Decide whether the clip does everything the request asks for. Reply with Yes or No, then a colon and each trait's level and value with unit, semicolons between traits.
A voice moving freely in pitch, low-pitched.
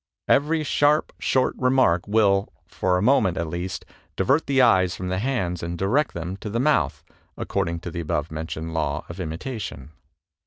Yes: wide, 7.2 semitones; very low, 95 Hz